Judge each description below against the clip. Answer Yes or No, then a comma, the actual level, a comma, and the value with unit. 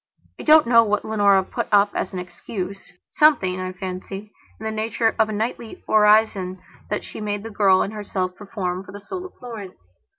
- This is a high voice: Yes, high, 205 Hz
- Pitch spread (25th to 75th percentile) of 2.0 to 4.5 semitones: Yes, average, 2.7 semitones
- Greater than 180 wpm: Yes, average, 190 wpm